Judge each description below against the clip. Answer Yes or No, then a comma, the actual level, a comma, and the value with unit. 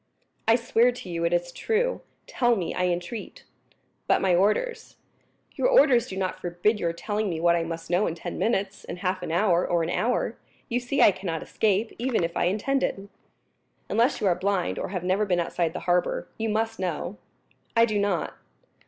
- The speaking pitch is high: Yes, high, 195 Hz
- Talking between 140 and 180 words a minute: No, average, 195 wpm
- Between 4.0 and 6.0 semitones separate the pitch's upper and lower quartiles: Yes, average, 4.4 semitones